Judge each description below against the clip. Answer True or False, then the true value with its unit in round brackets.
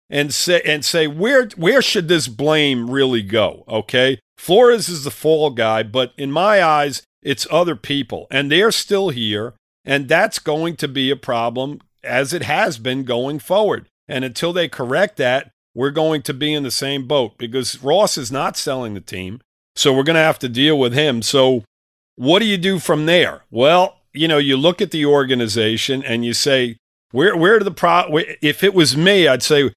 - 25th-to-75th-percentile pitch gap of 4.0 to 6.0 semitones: True (4.3 semitones)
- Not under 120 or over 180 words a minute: False (200 wpm)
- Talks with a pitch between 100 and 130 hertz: False (140 Hz)